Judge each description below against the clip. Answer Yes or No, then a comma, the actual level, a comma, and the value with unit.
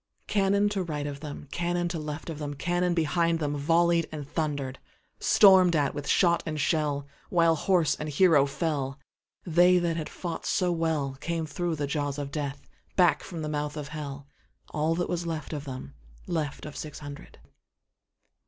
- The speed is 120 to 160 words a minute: Yes, average, 145 wpm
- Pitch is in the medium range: Yes, medium, 155 Hz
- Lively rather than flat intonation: No, average, 3.1 semitones